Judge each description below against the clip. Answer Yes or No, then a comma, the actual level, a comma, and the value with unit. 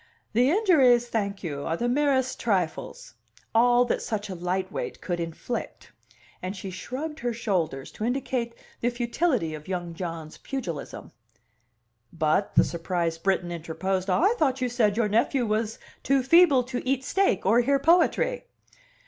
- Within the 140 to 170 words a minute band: Yes, average, 155 wpm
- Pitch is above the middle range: Yes, high, 230 Hz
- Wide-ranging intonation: Yes, wide, 6.3 semitones